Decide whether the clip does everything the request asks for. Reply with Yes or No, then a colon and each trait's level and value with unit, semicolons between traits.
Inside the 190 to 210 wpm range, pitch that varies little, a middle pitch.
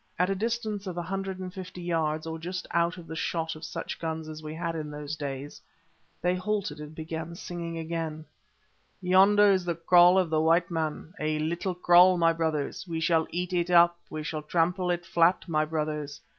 Yes: average, 200 wpm; narrow, 2.3 semitones; medium, 170 Hz